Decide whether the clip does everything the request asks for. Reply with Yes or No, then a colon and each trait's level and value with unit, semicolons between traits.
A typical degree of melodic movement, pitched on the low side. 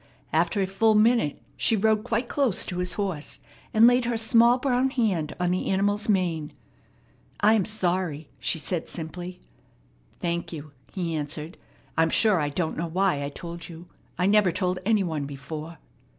No: average, 4.9 semitones; medium, 180 Hz